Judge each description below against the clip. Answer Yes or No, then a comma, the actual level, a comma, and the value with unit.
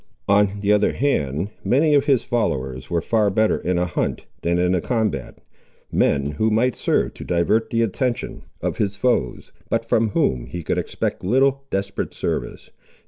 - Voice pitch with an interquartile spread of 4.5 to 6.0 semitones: Yes, average, 5.2 semitones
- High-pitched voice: No, low, 105 Hz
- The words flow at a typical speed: Yes, average, 175 wpm